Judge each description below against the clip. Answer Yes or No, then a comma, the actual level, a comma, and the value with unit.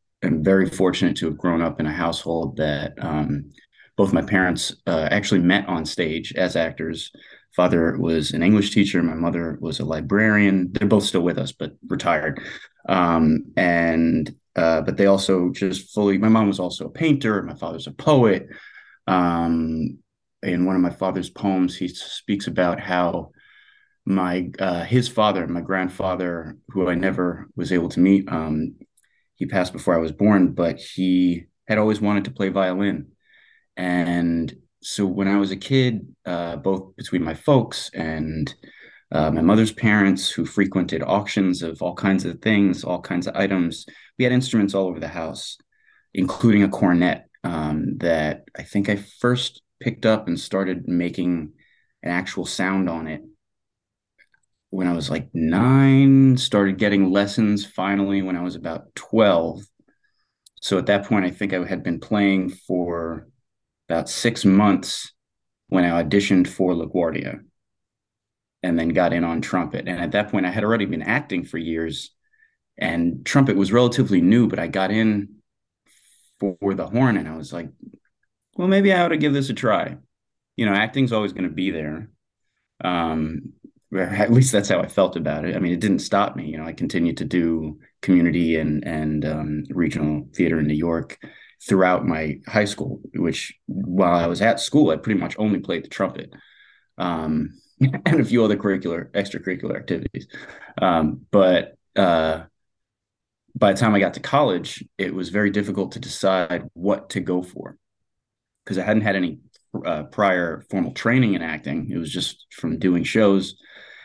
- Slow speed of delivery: No, average, 170 wpm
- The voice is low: Yes, very low, 95 Hz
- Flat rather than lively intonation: No, average, 3.4 semitones